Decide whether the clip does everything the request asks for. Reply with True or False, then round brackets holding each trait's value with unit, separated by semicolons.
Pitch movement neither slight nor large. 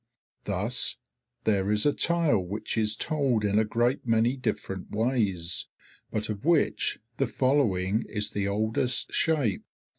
True (4.0 semitones)